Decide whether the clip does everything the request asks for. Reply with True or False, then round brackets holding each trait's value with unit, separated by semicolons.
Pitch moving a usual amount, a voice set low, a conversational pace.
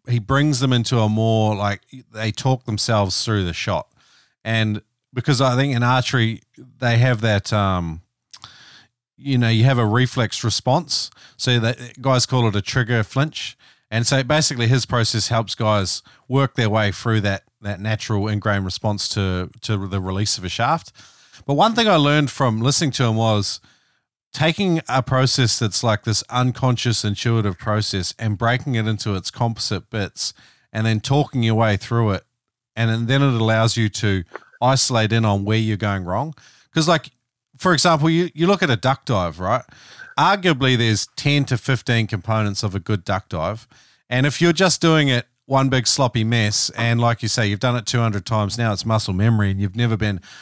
True (3.5 semitones; 115 Hz; 185 wpm)